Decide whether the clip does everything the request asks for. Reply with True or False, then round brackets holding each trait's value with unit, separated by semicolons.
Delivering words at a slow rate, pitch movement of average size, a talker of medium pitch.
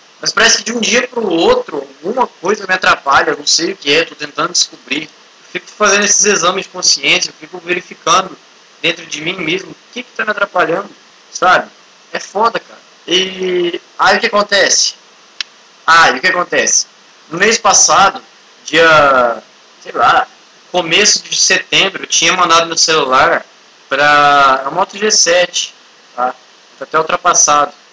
False (155 wpm; 4.6 semitones; 180 Hz)